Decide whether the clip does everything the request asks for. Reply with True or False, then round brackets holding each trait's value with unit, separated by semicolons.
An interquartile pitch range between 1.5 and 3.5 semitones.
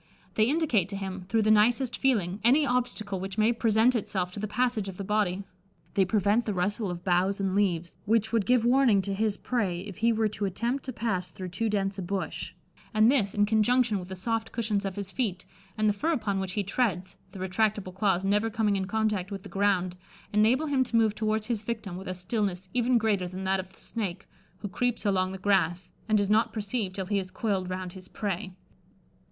True (2.9 semitones)